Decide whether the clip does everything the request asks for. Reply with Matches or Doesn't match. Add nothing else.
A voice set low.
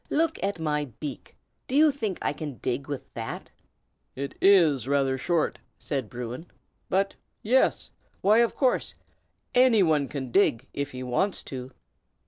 Doesn't match